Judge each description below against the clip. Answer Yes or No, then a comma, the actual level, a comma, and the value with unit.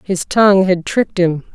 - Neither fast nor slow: Yes, average, 195 wpm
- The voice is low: No, medium, 185 Hz